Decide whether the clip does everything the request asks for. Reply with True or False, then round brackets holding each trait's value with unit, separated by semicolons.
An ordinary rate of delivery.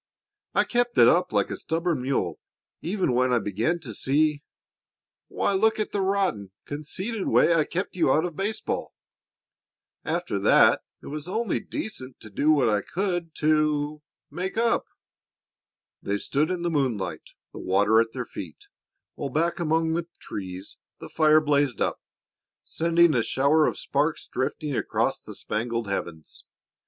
True (155 wpm)